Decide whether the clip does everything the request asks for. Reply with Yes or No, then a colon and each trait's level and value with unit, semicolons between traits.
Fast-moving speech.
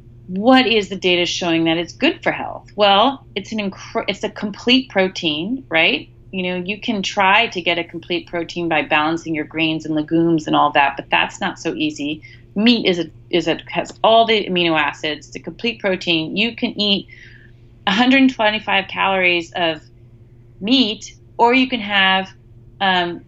No: average, 180 wpm